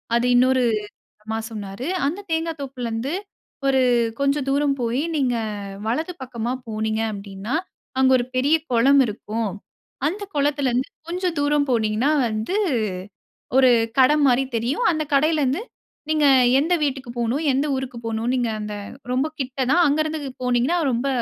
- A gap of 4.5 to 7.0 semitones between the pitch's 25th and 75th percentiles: No, average, 3.7 semitones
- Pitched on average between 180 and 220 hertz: No, very high, 260 Hz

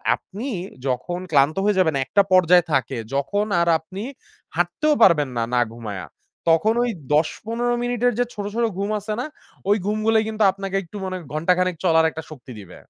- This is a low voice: No, medium, 185 Hz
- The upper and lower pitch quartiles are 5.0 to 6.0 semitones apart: Yes, wide, 5.6 semitones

